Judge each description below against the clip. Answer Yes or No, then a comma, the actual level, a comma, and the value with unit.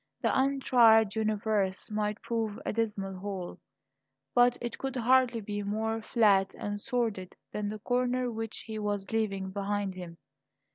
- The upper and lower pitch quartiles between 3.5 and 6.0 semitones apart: No, narrow, 2.5 semitones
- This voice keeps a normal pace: Yes, average, 145 wpm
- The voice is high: Yes, high, 215 Hz